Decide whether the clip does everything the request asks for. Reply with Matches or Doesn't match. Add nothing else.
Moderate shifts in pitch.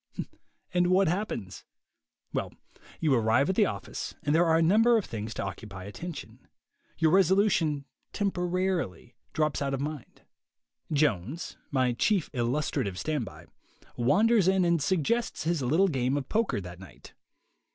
Doesn't match